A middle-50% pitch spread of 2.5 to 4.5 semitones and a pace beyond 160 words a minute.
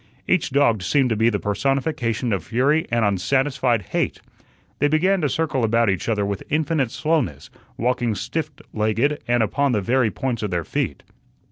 No: average, 5.0 semitones; average, 170 wpm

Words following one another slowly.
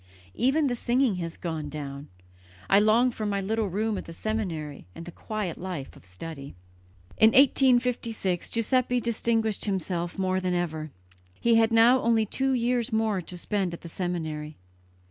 No: average, 165 wpm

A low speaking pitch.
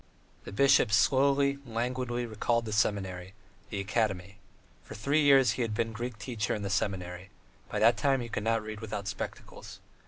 Yes: low, 110 Hz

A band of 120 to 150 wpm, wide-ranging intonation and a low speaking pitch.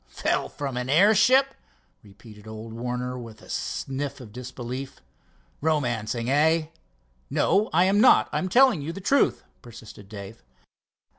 Yes: average, 140 wpm; wide, 6.5 semitones; low, 130 Hz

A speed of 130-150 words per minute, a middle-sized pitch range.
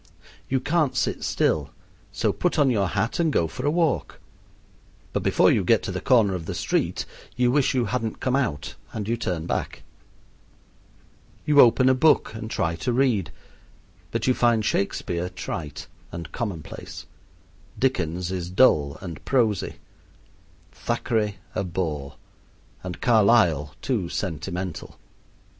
No: average, 145 wpm; wide, 6.5 semitones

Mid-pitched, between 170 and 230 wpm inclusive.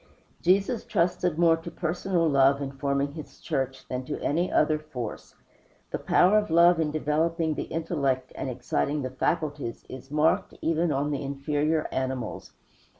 No: medium, 150 Hz; average, 155 wpm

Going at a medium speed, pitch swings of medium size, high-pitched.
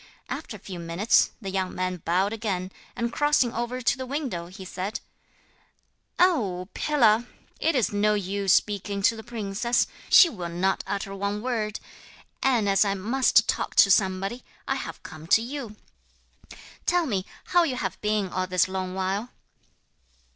Yes: average, 160 wpm; average, 4.1 semitones; high, 205 Hz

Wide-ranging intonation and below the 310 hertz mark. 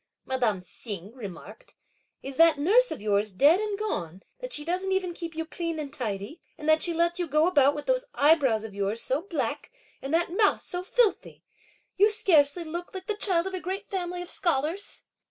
No: wide, 5.8 semitones; very high, 330 Hz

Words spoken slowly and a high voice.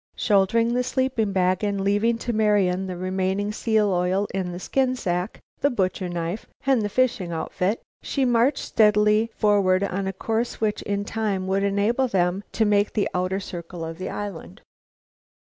No: average, 170 wpm; high, 200 Hz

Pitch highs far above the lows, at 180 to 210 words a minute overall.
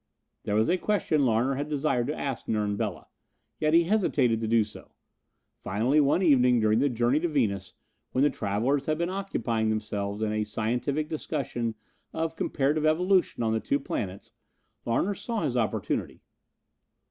No: wide, 5.8 semitones; average, 165 wpm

